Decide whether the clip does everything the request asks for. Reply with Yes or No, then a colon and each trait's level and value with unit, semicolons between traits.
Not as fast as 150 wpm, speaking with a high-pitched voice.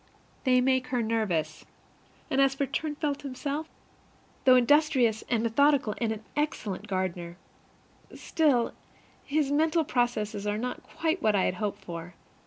Yes: average, 140 wpm; very high, 250 Hz